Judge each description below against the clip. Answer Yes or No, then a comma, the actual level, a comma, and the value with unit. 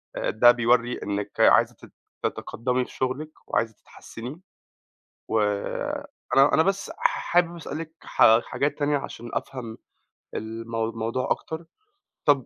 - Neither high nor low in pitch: No, low, 125 Hz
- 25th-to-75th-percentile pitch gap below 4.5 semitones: No, average, 4.8 semitones